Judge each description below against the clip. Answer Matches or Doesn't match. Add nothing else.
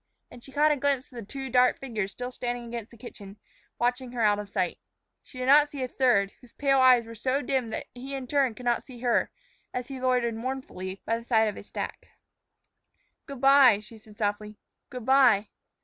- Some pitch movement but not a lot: Matches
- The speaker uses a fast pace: Matches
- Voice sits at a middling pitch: Doesn't match